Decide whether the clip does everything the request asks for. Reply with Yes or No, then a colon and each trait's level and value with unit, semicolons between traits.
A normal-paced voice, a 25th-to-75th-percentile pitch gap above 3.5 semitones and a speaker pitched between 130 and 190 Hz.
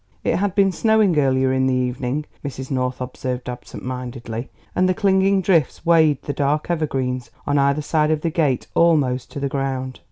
Yes: average, 185 wpm; average, 4.4 semitones; medium, 140 Hz